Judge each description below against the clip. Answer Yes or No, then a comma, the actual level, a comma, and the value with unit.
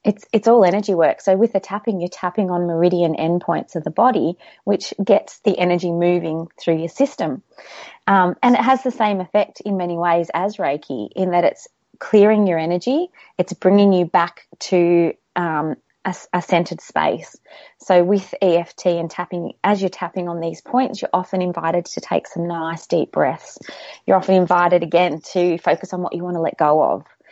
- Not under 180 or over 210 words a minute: Yes, average, 190 wpm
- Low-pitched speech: No, medium, 180 Hz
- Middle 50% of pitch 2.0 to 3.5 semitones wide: Yes, average, 2.8 semitones